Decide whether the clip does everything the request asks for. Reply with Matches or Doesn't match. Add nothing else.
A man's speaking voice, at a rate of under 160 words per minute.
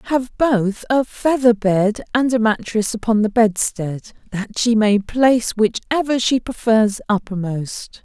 Doesn't match